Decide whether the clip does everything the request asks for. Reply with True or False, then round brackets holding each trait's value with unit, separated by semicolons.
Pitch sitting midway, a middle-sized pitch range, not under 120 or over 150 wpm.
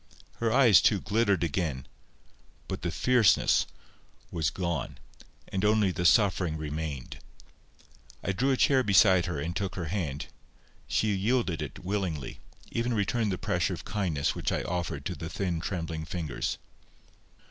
False (90 Hz; 4.2 semitones; 145 wpm)